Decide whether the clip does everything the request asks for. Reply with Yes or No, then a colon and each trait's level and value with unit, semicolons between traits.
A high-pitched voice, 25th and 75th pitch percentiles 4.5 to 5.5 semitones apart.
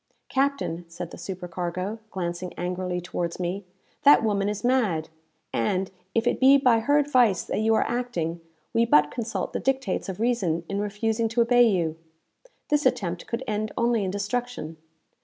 Yes: high, 205 Hz; average, 5.2 semitones